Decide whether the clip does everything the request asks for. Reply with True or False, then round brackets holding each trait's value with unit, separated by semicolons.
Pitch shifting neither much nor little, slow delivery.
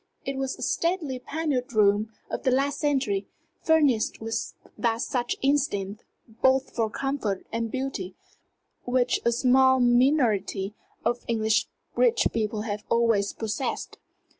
True (3.8 semitones; 130 wpm)